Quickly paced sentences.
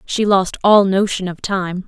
No: average, 190 wpm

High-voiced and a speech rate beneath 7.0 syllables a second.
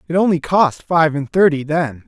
No: medium, 160 Hz; 4.8 syllables/s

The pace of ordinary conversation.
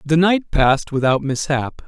Yes: average, 160 wpm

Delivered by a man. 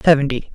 Yes: male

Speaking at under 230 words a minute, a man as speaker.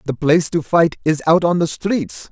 No: fast, 235 wpm; male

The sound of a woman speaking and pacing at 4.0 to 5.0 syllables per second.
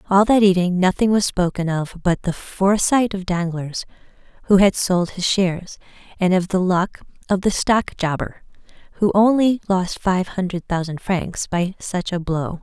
Yes: female; 4.6 syllables/s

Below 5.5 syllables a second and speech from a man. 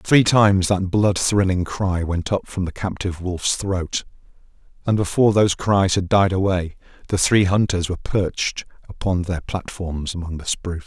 Yes: 4.9 syllables/s; male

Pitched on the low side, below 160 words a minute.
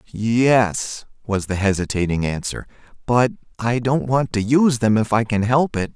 No: low, 115 Hz; average, 170 wpm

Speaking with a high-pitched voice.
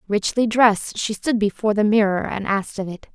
Yes: high, 210 Hz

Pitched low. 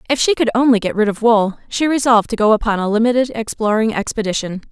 No: high, 225 Hz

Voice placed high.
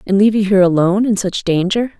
Yes: high, 200 Hz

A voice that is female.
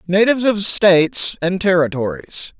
No: male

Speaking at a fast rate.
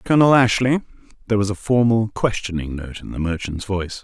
No: average, 180 wpm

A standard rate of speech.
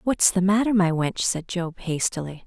Yes: average, 195 wpm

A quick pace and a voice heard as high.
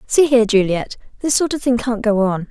Yes: fast, 240 wpm; high, 230 Hz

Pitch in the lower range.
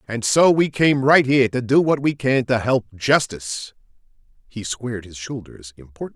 Yes: low, 120 Hz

